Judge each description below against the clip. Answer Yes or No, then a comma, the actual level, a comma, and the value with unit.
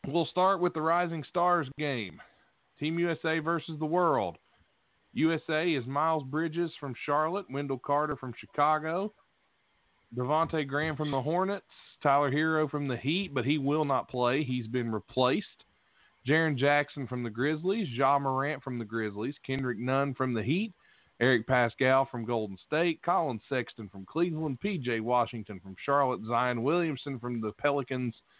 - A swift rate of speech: No, average, 155 wpm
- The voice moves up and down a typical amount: Yes, average, 4.2 semitones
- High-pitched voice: No, medium, 140 Hz